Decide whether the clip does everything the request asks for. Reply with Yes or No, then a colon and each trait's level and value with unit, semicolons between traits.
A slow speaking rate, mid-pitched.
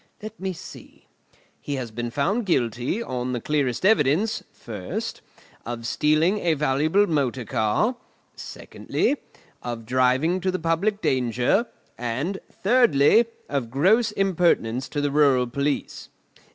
Yes: slow, 125 wpm; medium, 145 Hz